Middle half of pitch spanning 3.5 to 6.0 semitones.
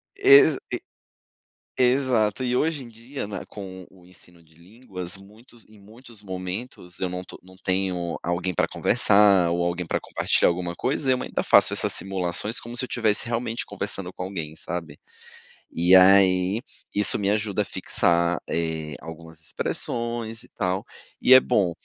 Yes: average, 4.7 semitones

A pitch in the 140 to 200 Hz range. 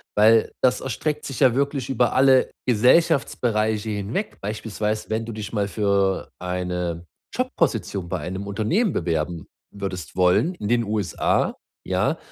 No: low, 105 Hz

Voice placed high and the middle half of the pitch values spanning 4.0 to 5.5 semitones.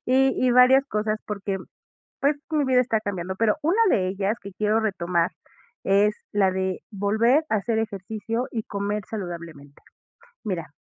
No: high, 210 Hz; average, 3.5 semitones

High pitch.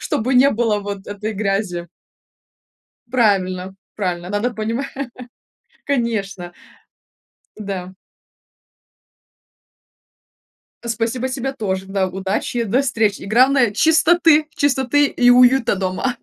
Yes: high, 220 Hz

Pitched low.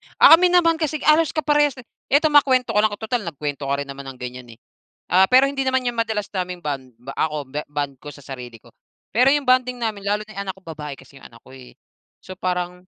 No: high, 190 Hz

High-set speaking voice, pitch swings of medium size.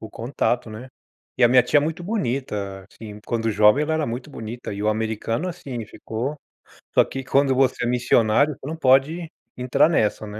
No: low, 125 Hz; average, 4.5 semitones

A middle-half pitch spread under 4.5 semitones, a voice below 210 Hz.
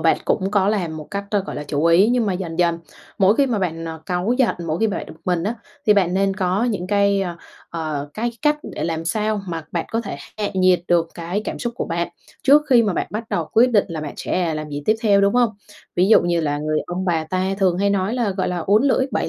Yes: average, 3.9 semitones; medium, 185 Hz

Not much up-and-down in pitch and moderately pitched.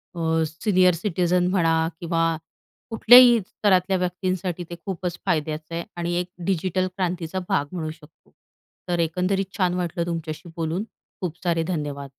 Yes: narrow, 2.2 semitones; medium, 175 Hz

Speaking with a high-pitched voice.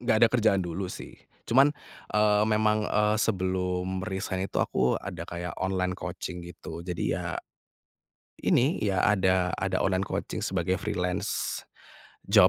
No: very low, 95 Hz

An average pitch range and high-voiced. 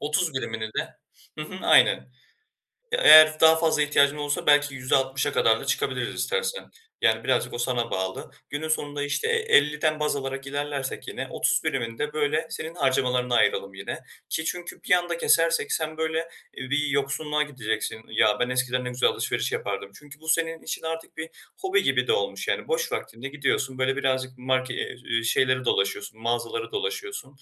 No: average, 3.9 semitones; medium, 145 Hz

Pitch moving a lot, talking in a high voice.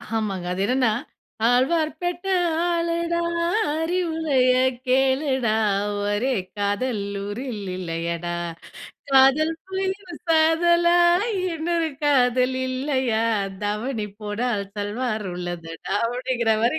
Yes: wide, 7.2 semitones; very high, 255 Hz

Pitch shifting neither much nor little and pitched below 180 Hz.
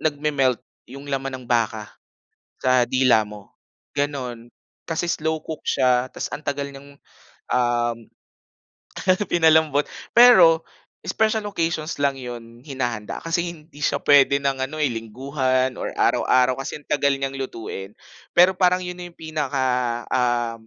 Yes: average, 4.0 semitones; low, 135 Hz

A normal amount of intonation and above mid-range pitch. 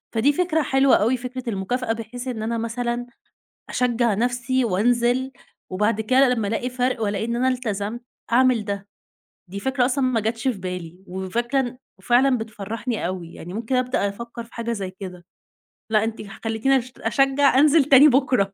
Yes: average, 3.3 semitones; high, 235 Hz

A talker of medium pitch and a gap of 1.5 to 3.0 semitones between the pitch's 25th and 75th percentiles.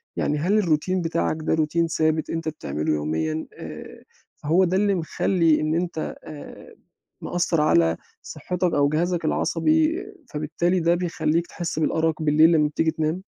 Yes: medium, 160 Hz; narrow, 2.4 semitones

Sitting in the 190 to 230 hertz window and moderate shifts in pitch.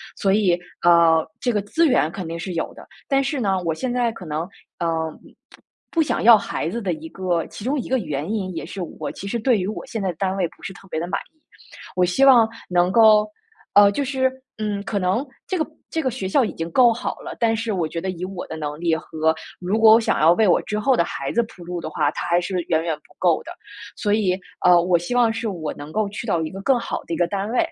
Yes: high, 195 Hz; average, 4.9 semitones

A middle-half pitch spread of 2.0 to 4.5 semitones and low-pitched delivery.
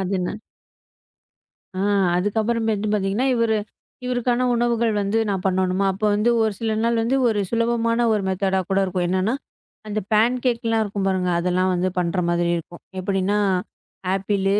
No: average, 3.5 semitones; high, 205 Hz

